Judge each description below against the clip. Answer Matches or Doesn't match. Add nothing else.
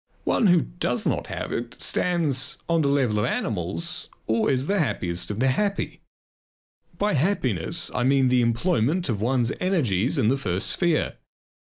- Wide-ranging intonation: Matches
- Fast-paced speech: Doesn't match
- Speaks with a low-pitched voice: Matches